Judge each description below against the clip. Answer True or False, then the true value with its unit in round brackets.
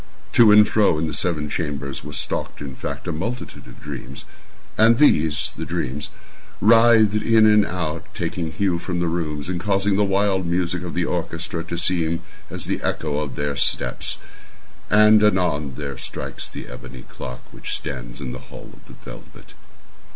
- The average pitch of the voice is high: False (85 Hz)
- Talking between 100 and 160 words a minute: False (170 wpm)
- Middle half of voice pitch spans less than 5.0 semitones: False (5.5 semitones)